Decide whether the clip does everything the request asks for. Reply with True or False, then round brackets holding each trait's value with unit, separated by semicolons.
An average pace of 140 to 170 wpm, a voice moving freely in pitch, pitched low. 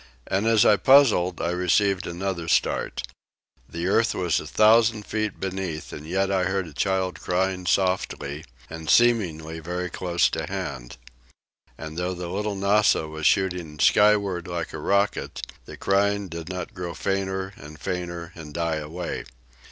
False (155 wpm; 2.8 semitones; 90 Hz)